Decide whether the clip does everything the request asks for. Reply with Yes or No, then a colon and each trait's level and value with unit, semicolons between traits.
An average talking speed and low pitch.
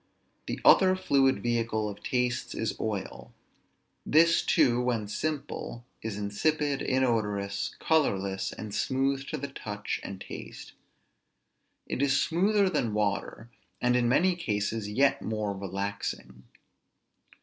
No: slow, 120 wpm; low, 120 Hz